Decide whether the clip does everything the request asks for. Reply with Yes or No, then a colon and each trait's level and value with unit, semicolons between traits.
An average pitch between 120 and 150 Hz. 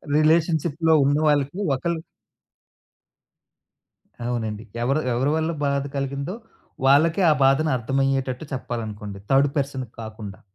Yes: low, 135 Hz